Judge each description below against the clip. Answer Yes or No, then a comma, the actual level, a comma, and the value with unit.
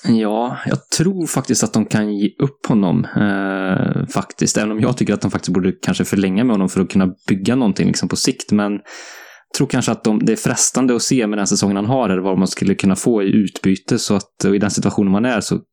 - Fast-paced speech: Yes, fast, 245 wpm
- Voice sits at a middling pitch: No, low, 105 Hz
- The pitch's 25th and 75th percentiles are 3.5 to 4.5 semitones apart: No, average, 3.0 semitones